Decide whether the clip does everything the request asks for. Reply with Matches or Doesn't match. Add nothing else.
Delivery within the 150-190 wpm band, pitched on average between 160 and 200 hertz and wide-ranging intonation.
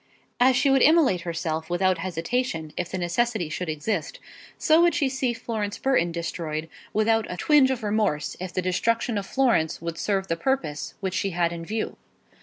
Matches